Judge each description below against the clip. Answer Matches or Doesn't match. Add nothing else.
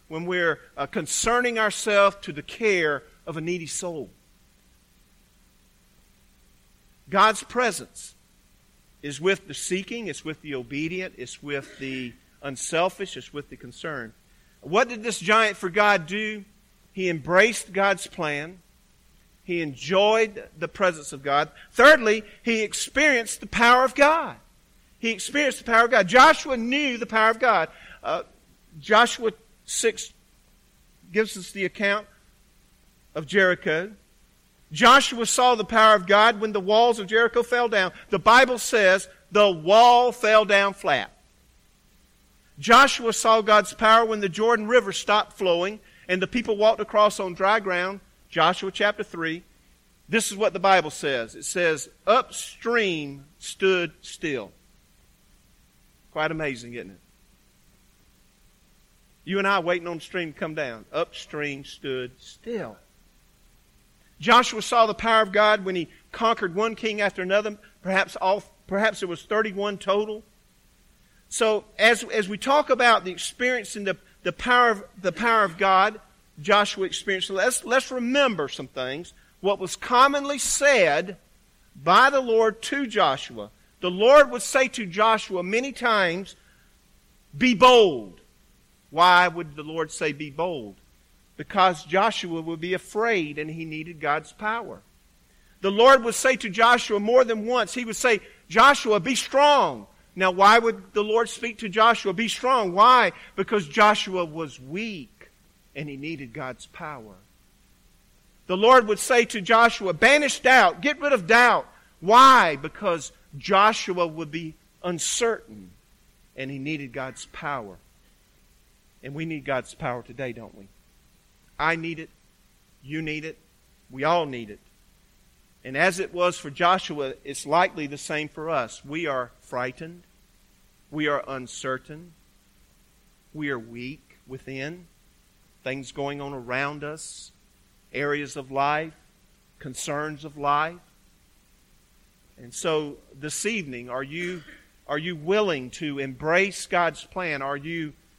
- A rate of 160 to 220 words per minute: Doesn't match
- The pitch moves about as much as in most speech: Doesn't match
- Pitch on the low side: Doesn't match